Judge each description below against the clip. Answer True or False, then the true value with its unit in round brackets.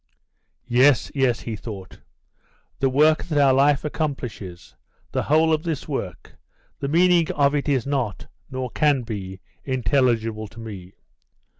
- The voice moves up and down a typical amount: True (4.7 semitones)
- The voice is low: True (130 Hz)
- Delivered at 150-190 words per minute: False (140 wpm)